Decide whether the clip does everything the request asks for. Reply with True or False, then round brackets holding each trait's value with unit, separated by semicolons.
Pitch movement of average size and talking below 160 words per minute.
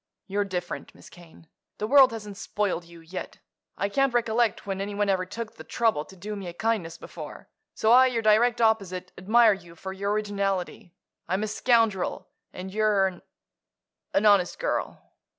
False (3.2 semitones; 170 wpm)